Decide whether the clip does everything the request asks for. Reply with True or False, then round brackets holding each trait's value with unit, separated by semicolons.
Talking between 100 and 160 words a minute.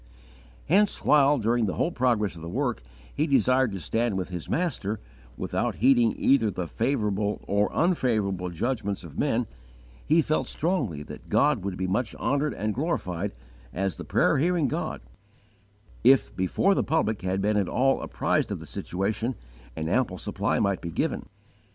False (170 wpm)